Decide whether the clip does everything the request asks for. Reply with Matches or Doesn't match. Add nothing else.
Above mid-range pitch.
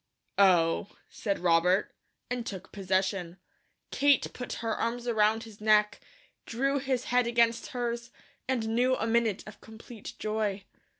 Matches